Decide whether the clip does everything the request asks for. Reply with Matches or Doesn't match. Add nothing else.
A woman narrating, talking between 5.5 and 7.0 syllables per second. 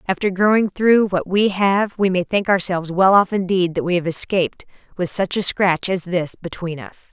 Doesn't match